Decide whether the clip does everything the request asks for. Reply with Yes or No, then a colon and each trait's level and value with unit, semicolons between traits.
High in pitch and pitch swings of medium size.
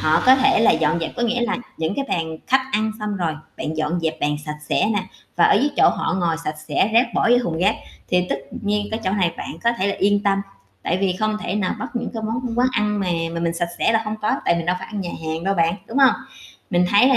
Yes: high, 200 Hz; average, 4.9 semitones